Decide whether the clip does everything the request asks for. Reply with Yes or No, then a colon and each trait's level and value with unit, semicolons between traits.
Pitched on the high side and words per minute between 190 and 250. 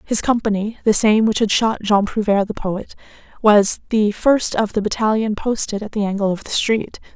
Yes: high, 210 Hz; average, 200 wpm